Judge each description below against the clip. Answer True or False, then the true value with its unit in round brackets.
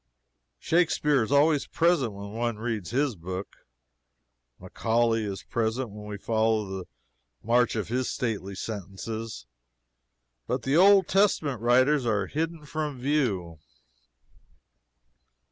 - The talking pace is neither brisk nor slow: False (115 wpm)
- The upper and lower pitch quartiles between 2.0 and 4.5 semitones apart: False (5.4 semitones)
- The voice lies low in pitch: True (115 Hz)